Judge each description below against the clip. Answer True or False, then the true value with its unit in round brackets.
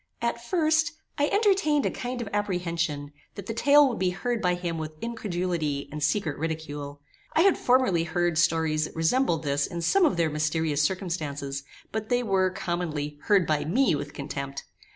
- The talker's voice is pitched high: False (175 Hz)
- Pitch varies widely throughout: True (7.4 semitones)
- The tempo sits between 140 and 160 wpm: False (175 wpm)